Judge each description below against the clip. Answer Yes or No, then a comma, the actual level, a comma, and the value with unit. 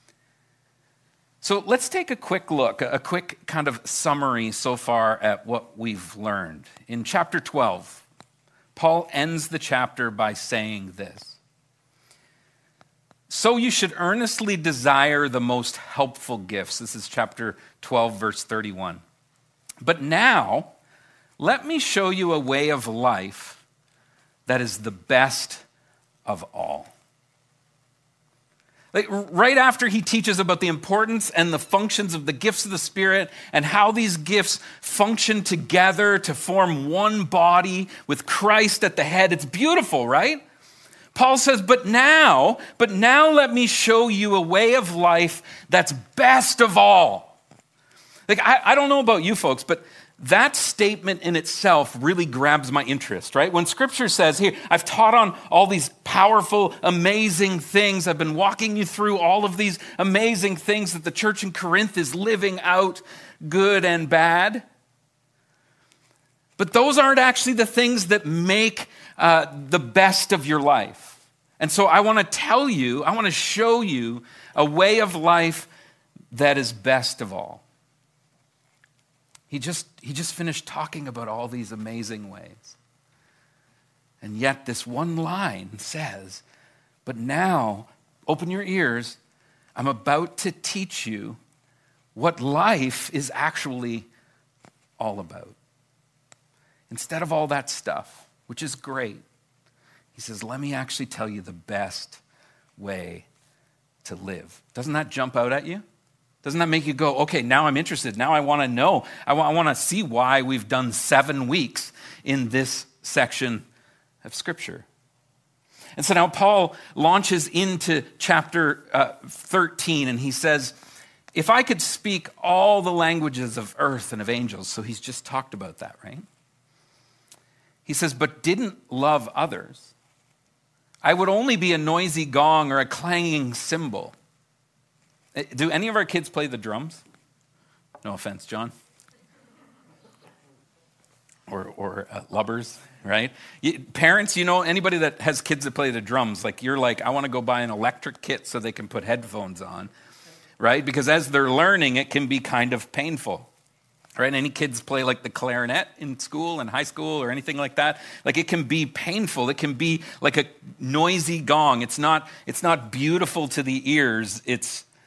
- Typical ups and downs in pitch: No, wide, 5.8 semitones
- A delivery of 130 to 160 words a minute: Yes, average, 155 wpm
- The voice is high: No, medium, 150 Hz